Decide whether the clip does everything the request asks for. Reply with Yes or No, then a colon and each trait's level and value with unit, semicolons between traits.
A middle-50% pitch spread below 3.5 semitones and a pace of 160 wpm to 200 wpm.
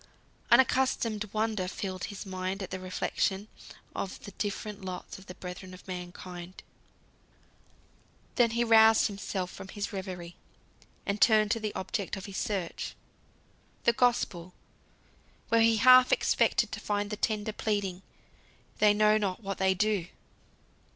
No: narrow, 2.6 semitones; average, 140 wpm